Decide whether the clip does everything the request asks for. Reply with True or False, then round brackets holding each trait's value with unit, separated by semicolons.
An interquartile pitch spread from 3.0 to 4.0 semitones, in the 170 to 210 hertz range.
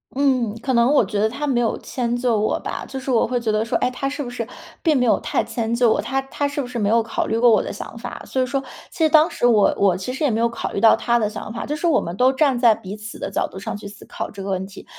False (3.5 semitones; 240 Hz)